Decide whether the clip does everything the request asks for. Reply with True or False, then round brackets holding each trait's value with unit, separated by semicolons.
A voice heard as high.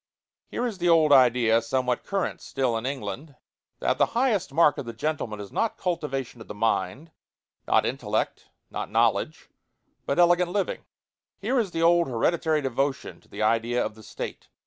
False (140 Hz)